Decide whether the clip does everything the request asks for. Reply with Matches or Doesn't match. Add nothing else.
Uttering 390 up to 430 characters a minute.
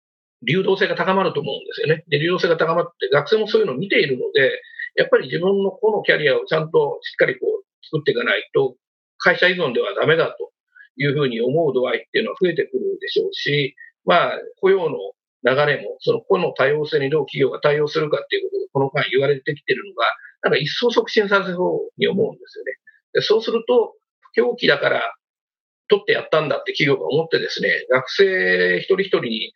Matches